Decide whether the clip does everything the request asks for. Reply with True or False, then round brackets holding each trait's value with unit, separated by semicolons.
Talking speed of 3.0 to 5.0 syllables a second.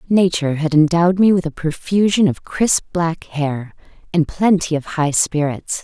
True (4.6 syllables/s)